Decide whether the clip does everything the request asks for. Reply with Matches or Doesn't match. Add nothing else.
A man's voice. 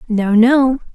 Doesn't match